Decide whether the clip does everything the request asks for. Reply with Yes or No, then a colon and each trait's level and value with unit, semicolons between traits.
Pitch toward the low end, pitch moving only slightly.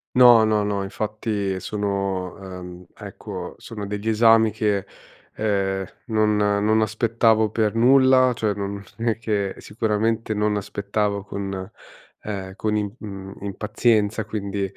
Yes: low, 105 Hz; narrow, 1.9 semitones